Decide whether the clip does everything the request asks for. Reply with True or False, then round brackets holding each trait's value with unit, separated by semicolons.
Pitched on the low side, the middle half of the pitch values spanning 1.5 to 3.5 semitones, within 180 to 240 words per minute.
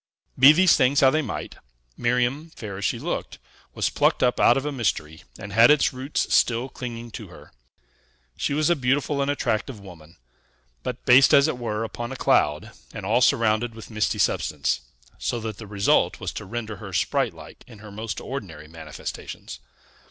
False (120 Hz; 4.0 semitones; 185 wpm)